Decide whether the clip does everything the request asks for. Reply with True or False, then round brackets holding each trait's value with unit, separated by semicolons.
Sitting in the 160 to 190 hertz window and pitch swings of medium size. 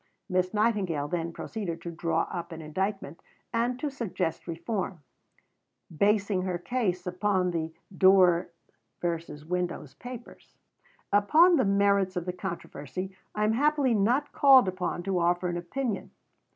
True (185 Hz; 3.7 semitones)